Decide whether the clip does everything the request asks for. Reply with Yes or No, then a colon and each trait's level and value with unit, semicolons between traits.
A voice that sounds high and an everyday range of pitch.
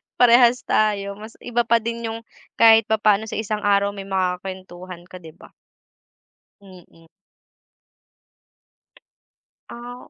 Yes: high, 210 Hz; average, 3.4 semitones